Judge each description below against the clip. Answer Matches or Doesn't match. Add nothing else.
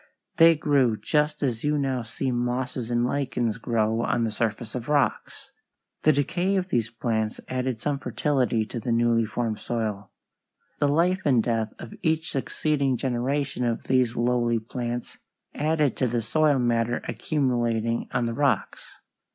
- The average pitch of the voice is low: Matches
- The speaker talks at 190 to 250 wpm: Doesn't match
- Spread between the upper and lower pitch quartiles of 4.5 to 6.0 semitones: Doesn't match